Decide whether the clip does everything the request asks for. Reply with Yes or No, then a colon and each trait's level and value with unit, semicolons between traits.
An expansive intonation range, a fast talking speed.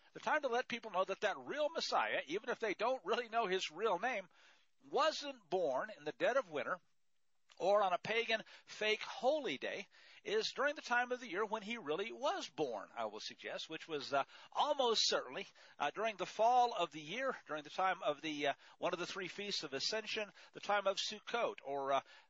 Yes: wide, 5.8 semitones; fast, 215 wpm